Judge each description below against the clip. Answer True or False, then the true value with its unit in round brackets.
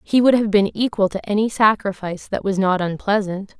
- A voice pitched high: True (205 Hz)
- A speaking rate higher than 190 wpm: True (200 wpm)